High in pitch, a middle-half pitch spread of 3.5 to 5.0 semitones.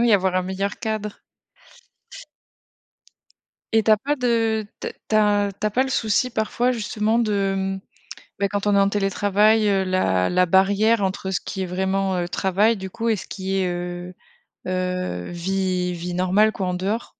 No: high, 195 Hz; narrow, 2.6 semitones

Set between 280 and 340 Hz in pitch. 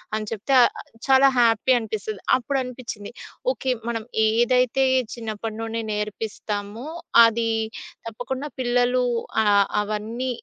No: high, 230 Hz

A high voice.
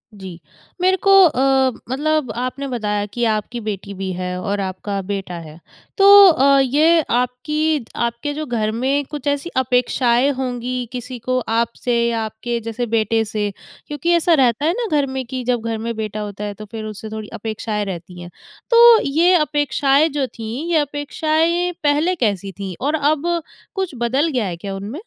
Yes: very high, 250 Hz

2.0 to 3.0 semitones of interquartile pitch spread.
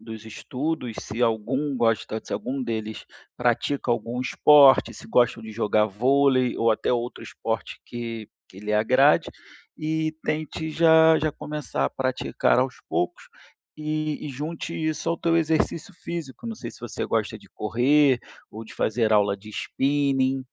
No: average, 5.1 semitones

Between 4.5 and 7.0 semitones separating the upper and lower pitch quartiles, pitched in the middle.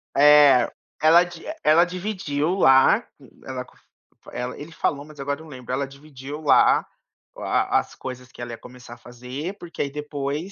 No: average, 3.4 semitones; medium, 145 Hz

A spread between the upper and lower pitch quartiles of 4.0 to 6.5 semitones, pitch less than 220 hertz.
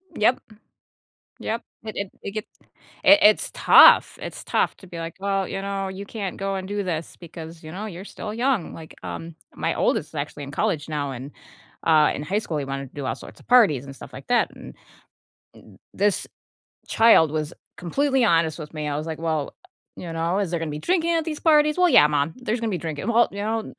Yes: wide, 5.6 semitones; medium, 185 Hz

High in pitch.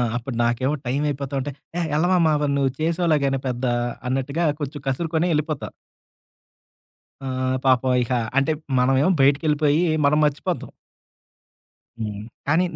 No: medium, 140 Hz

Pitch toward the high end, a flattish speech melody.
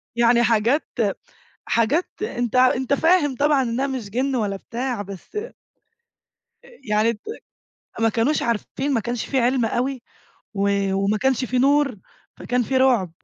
No: high, 245 Hz; average, 3.3 semitones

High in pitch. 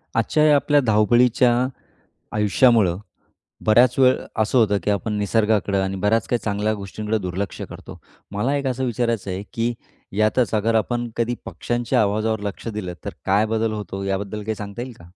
No: low, 110 Hz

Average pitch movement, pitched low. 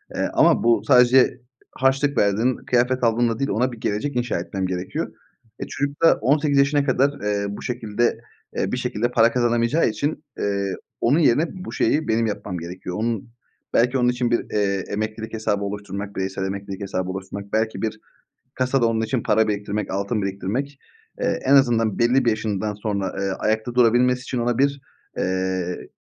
Yes: average, 3.9 semitones; low, 115 Hz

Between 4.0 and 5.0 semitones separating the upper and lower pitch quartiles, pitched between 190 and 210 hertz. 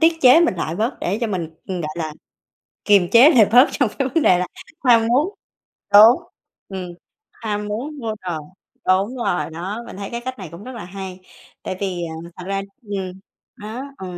Yes: average, 4.7 semitones; high, 205 Hz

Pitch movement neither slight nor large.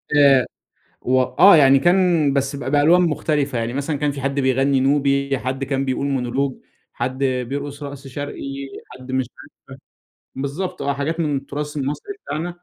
No: narrow, 1.6 semitones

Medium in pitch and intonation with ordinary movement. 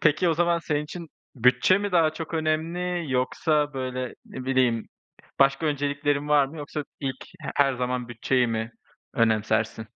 Yes: medium, 145 Hz; average, 3.9 semitones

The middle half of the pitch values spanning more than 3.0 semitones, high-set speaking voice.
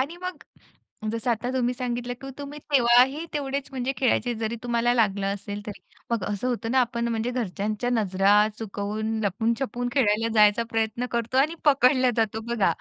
No: average, 2.7 semitones; high, 235 Hz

